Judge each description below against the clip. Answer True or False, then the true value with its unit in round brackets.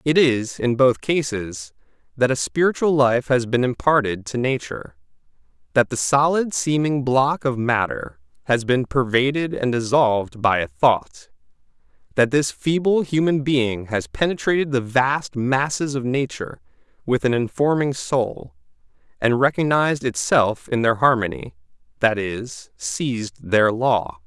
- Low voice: True (125 Hz)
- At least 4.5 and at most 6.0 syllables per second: False (4.3 syllables/s)